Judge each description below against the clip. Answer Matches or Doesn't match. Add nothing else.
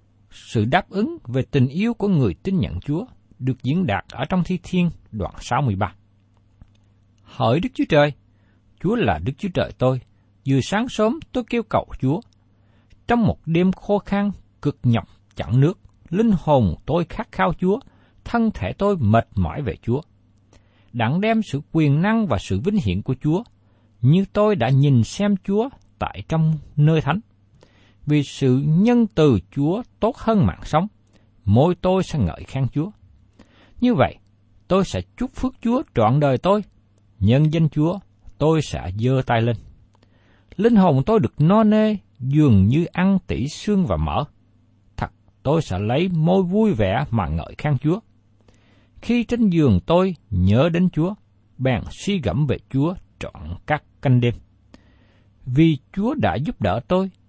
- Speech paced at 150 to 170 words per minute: Matches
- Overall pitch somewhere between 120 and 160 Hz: Matches